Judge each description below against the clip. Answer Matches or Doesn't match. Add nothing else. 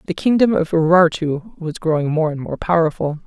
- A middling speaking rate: Matches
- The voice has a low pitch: Doesn't match